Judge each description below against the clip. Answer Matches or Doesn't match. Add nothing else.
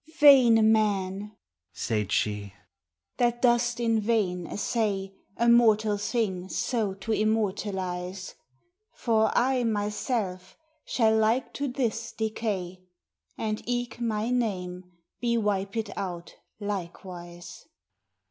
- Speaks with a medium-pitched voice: Doesn't match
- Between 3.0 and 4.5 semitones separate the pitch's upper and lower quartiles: Matches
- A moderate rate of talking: Doesn't match